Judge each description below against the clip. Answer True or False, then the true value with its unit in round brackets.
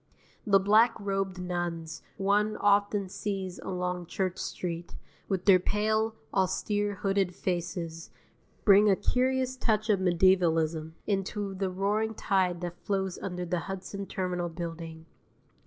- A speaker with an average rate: False (125 wpm)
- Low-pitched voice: False (190 Hz)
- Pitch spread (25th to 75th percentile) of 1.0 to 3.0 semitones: True (2.5 semitones)